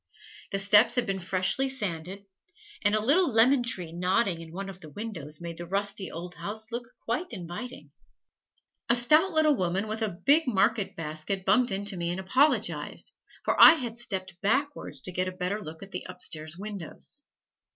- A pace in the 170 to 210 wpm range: Yes, average, 180 wpm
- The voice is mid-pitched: No, high, 195 Hz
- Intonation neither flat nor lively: Yes, average, 4.9 semitones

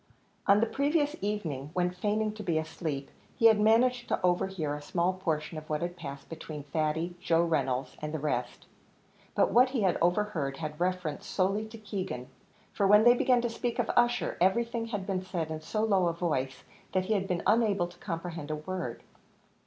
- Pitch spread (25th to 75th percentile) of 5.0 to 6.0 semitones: Yes, average, 5.3 semitones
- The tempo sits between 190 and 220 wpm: Yes, average, 195 wpm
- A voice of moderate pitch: Yes, medium, 180 Hz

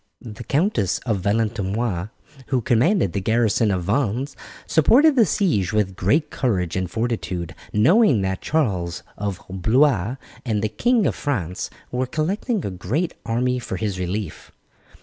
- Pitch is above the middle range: No, low, 110 Hz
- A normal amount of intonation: No, wide, 6.7 semitones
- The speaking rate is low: No, average, 145 wpm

